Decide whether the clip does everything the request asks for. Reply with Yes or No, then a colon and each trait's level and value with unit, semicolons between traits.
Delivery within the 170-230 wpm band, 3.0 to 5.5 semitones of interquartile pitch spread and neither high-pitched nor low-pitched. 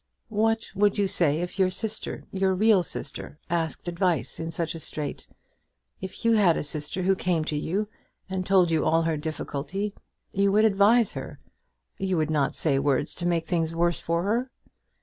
Yes: average, 185 wpm; average, 3.6 semitones; medium, 175 Hz